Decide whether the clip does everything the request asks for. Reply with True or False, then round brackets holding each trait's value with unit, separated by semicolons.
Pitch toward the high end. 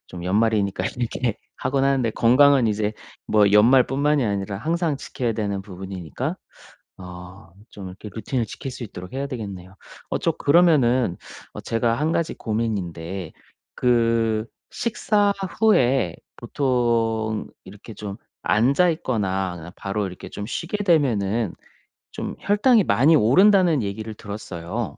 False (115 Hz)